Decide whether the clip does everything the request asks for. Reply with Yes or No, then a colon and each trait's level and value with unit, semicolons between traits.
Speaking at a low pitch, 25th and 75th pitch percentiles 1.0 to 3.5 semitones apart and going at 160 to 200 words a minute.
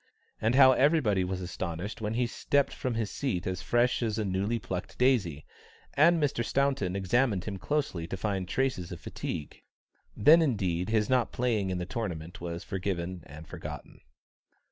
No: low, 105 Hz; wide, 5.6 semitones; average, 165 wpm